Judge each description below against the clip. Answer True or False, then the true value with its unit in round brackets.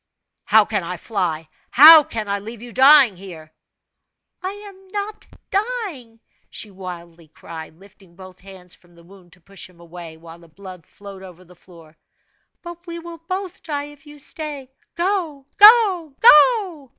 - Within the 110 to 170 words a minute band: True (160 wpm)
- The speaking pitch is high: True (225 Hz)